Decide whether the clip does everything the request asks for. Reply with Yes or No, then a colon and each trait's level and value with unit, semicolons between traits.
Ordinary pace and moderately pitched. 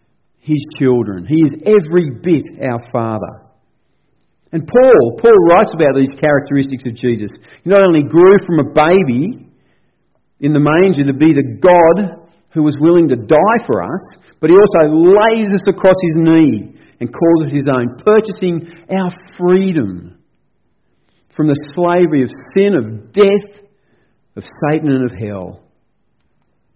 Yes: average, 150 wpm; medium, 160 Hz